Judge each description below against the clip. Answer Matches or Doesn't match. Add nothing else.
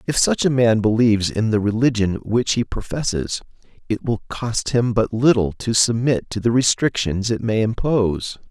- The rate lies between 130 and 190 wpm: Matches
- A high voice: Doesn't match